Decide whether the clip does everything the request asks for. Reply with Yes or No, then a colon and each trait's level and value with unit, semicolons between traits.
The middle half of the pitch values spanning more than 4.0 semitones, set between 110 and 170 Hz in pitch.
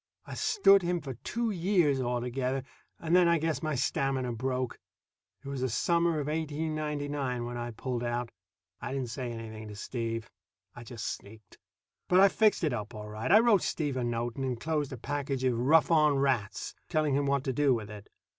Yes: average, 4.4 semitones; low, 135 Hz